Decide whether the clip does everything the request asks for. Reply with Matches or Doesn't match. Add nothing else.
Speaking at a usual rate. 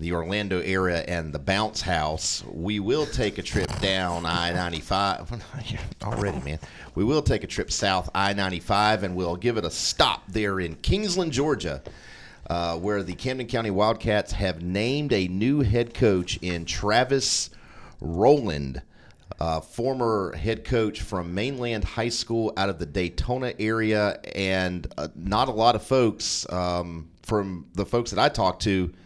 Matches